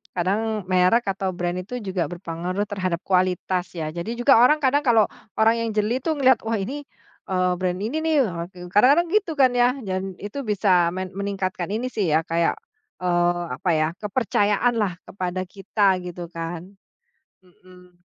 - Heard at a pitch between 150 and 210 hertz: Yes, high, 190 Hz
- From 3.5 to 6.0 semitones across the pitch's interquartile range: Yes, average, 4.2 semitones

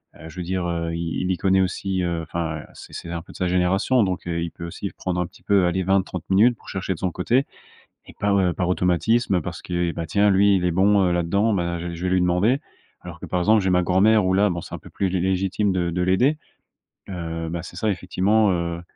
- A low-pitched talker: Yes, very low, 90 Hz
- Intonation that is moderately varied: No, narrow, 2.2 semitones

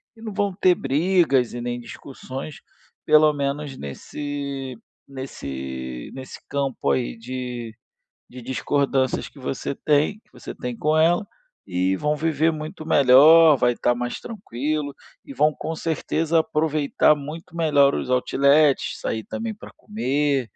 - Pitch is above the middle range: No, medium, 140 Hz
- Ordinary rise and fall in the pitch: Yes, average, 3.6 semitones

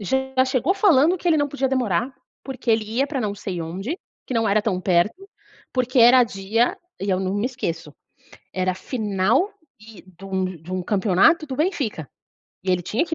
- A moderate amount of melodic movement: No, wide, 5.9 semitones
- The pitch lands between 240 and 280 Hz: No, high, 220 Hz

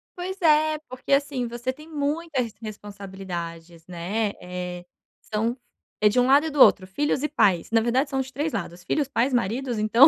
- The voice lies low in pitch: No, high, 240 Hz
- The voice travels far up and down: Yes, wide, 6.5 semitones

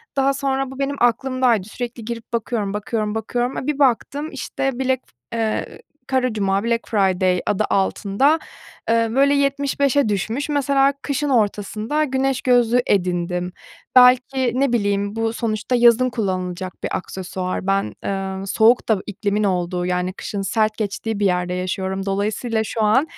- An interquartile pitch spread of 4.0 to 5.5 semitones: Yes, average, 4.8 semitones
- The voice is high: Yes, high, 225 Hz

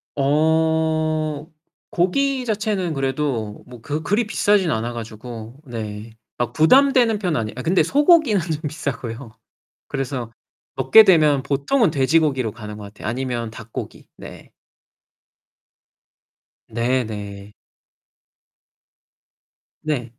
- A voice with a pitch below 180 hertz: Yes, medium, 140 Hz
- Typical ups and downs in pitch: No, wide, 6.3 semitones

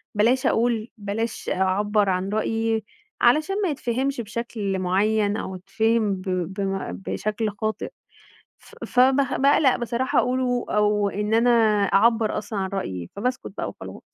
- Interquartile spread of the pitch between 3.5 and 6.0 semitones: No, average, 3.0 semitones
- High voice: Yes, high, 215 Hz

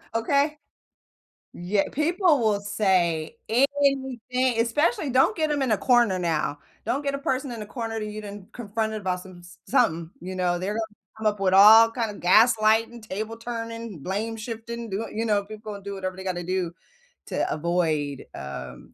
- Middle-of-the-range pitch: No, high, 215 Hz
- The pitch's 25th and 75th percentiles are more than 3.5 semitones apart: Yes, average, 4.2 semitones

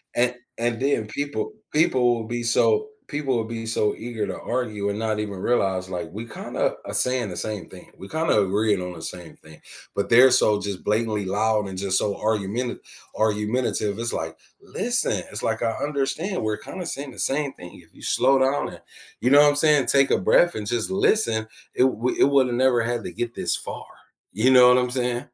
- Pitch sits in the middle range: No, low, 115 Hz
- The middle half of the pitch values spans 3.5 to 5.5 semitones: Yes, average, 3.9 semitones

